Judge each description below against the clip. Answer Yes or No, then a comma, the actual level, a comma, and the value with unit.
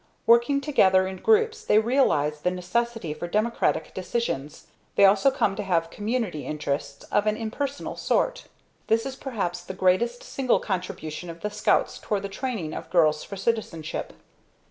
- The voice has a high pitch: Yes, high, 205 Hz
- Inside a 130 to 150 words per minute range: No, average, 160 wpm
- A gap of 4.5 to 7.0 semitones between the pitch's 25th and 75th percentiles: Yes, average, 5.3 semitones